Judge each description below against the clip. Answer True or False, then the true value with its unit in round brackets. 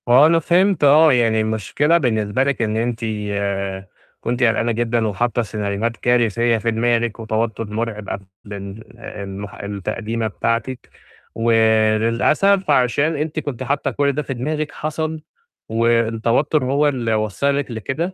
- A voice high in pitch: False (115 Hz)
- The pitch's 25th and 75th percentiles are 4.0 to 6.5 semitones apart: True (4.3 semitones)